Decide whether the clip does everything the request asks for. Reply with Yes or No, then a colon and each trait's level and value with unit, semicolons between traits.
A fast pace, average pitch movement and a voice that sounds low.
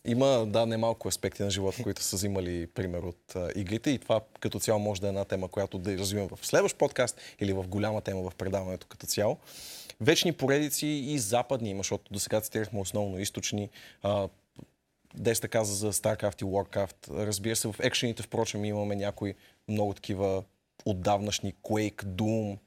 No: fast, 175 wpm; narrow, 2.1 semitones; low, 105 Hz